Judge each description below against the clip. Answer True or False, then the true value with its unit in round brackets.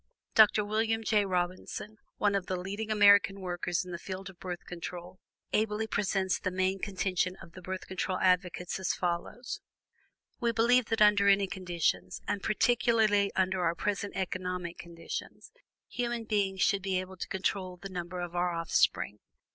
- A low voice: False (190 Hz)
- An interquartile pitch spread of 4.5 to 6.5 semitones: False (2.5 semitones)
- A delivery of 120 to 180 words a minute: True (165 wpm)